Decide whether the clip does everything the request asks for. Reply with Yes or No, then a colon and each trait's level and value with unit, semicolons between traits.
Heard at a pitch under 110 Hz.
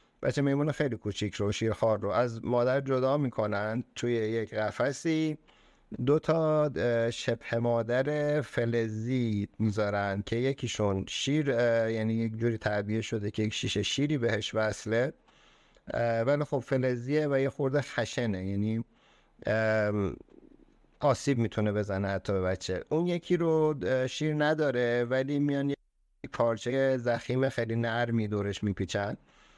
No: low, 115 Hz